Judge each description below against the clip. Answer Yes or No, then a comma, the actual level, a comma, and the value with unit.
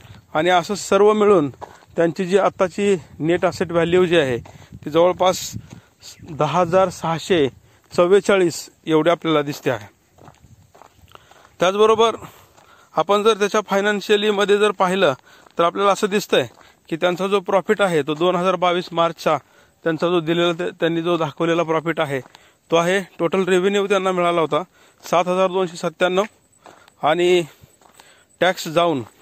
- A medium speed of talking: No, fast, 140 wpm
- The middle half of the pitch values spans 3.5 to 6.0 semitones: No, average, 3.1 semitones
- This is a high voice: No, medium, 175 Hz